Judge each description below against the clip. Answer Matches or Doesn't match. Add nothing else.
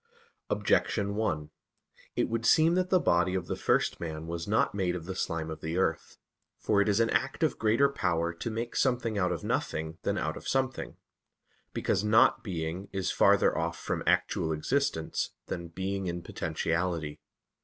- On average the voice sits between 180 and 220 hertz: Doesn't match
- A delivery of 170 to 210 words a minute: Matches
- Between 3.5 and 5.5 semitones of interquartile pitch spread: Matches